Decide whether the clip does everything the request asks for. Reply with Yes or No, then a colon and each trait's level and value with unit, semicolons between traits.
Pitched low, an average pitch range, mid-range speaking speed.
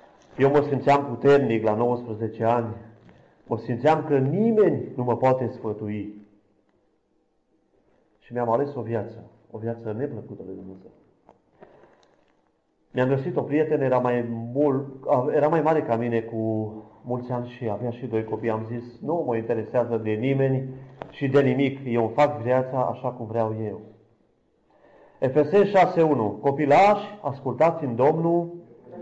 Yes: low, 125 Hz; average, 3.8 semitones; average, 140 wpm